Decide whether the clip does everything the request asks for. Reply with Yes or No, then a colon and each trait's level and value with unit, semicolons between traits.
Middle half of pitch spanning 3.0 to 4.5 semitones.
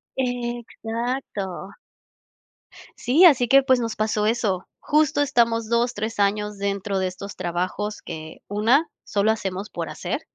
Yes: average, 3.5 semitones